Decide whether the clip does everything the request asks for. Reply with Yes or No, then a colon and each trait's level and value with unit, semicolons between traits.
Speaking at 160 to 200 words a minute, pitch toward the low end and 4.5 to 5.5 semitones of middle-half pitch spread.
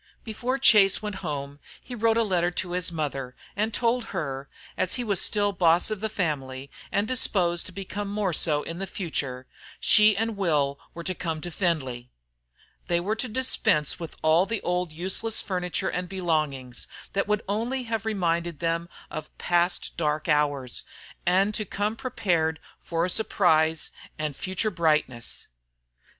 No: average, 165 wpm; medium, 175 Hz; average, 4.9 semitones